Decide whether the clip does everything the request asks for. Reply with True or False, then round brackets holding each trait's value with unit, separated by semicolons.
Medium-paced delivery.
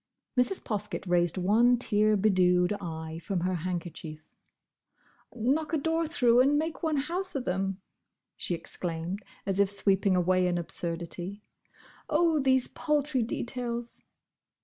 False (130 wpm)